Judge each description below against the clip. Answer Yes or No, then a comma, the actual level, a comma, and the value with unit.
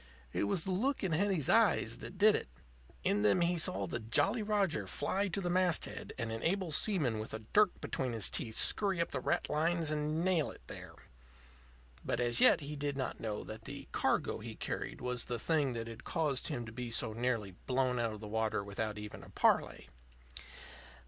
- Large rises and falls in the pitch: Yes, wide, 7.7 semitones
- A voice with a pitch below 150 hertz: Yes, low, 135 Hz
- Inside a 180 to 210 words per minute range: Yes, average, 200 wpm